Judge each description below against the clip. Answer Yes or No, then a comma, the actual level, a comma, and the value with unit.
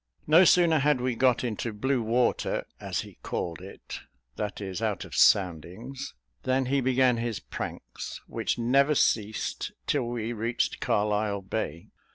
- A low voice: Yes, low, 120 Hz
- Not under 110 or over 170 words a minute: Yes, average, 150 wpm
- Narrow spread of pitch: No, average, 4.0 semitones